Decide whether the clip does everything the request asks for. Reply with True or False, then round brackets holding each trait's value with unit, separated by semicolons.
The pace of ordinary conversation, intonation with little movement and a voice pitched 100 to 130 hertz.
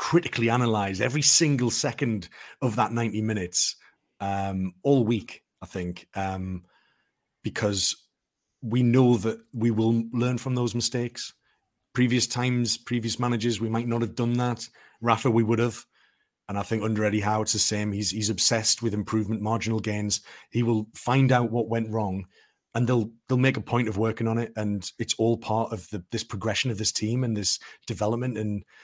True (180 wpm; 2.1 semitones; 115 Hz)